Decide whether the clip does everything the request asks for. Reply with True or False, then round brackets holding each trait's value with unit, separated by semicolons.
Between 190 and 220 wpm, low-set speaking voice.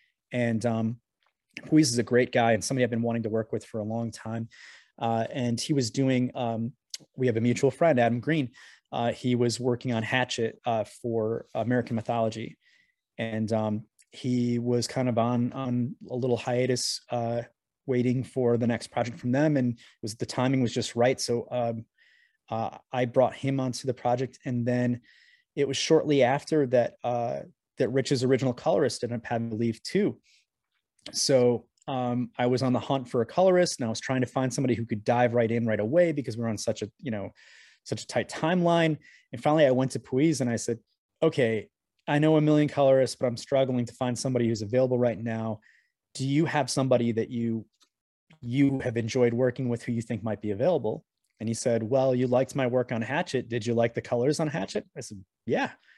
True (205 wpm; 125 Hz)